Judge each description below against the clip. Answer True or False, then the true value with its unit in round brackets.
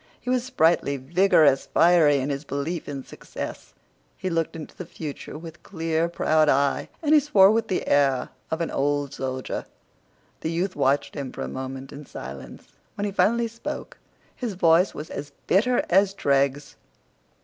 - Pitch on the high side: False (160 Hz)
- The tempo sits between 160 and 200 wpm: True (170 wpm)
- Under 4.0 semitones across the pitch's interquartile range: False (5.1 semitones)